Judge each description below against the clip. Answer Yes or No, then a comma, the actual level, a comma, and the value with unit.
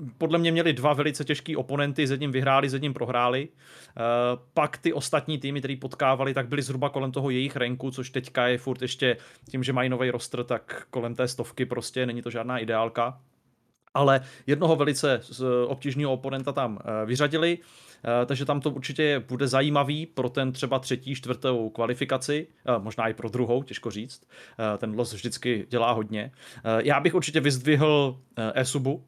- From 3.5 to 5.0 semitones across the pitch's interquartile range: No, average, 2.7 semitones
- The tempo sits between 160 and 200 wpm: Yes, average, 165 wpm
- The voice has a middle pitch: No, low, 130 Hz